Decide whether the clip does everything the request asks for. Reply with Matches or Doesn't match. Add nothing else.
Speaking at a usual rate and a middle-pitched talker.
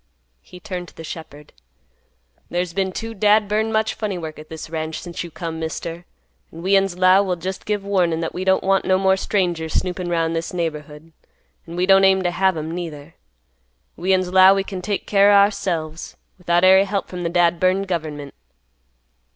Matches